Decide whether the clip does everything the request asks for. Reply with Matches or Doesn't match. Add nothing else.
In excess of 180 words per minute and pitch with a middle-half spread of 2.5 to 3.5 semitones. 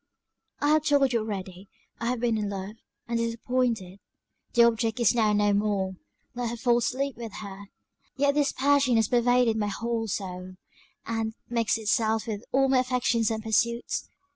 Doesn't match